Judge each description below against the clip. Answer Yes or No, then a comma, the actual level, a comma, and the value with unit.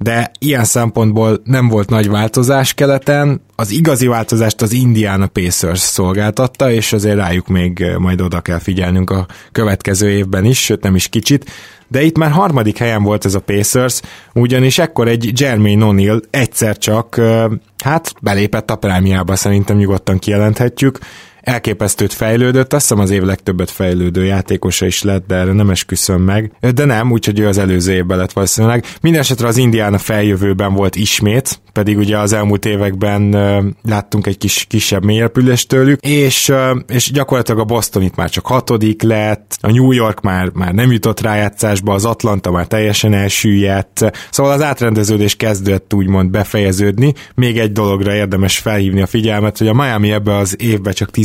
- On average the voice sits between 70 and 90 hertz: No, low, 105 Hz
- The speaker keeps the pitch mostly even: No, average, 3.1 semitones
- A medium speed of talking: No, fast, 165 wpm